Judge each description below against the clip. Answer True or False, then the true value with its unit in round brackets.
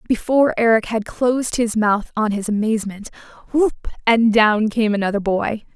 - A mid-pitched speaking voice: False (220 Hz)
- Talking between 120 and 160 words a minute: True (155 wpm)